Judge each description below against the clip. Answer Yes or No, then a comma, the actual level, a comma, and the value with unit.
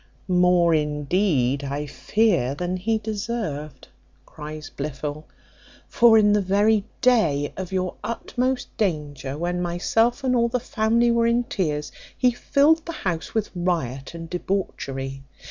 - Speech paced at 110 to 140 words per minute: Yes, slow, 135 wpm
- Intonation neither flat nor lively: No, wide, 7.0 semitones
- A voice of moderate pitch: Yes, medium, 180 Hz